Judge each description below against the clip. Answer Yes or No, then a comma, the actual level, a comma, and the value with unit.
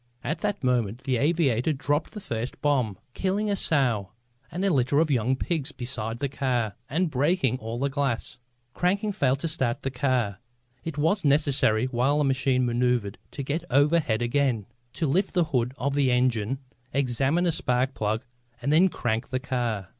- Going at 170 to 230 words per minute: Yes, average, 175 wpm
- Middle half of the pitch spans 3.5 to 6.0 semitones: Yes, average, 3.8 semitones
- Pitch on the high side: No, low, 135 Hz